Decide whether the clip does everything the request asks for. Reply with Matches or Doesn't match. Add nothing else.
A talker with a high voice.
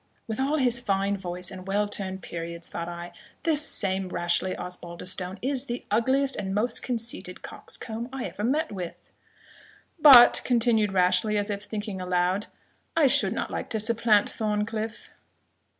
Matches